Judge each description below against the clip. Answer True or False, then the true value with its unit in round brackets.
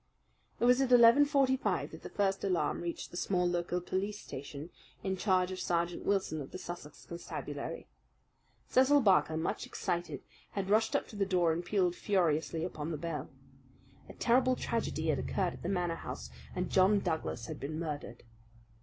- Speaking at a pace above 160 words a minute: True (180 wpm)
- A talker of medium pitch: True (180 Hz)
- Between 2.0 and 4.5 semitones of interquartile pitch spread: True (3.6 semitones)